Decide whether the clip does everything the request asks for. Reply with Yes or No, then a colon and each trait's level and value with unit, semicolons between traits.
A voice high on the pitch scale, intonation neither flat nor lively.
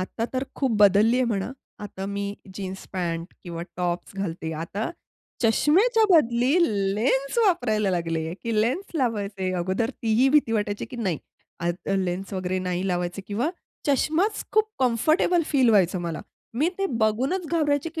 No: high, 215 Hz; wide, 6.3 semitones